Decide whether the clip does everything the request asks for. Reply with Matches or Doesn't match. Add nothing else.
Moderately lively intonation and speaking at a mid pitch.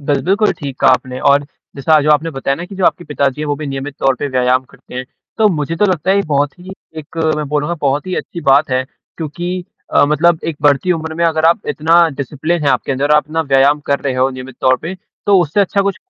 Matches